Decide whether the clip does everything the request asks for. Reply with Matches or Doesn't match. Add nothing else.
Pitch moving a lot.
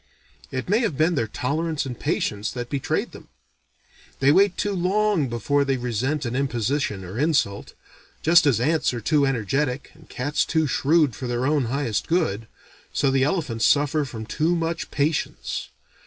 Doesn't match